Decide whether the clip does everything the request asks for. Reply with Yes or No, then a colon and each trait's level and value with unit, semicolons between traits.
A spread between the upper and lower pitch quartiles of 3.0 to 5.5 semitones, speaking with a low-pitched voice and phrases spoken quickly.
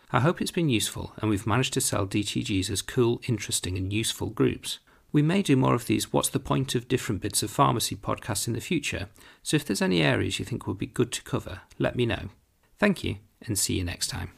Yes: average, 4.1 semitones; low, 110 Hz; fast, 240 wpm